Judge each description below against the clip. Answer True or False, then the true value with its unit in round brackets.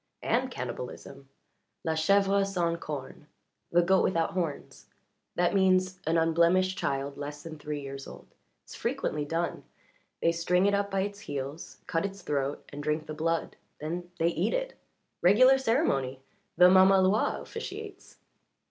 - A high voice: False (170 Hz)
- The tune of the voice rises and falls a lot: False (4.4 semitones)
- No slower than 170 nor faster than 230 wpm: False (150 wpm)